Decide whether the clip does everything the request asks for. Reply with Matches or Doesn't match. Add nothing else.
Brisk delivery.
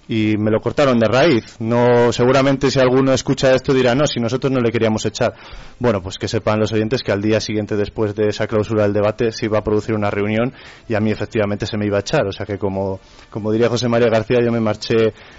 Matches